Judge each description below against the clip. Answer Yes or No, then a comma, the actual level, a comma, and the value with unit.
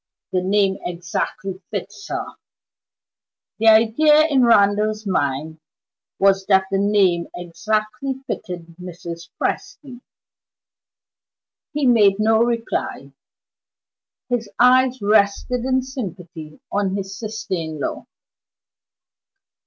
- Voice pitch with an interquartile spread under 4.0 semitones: No, average, 4.4 semitones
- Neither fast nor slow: No, slow, 100 wpm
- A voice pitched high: Yes, high, 205 Hz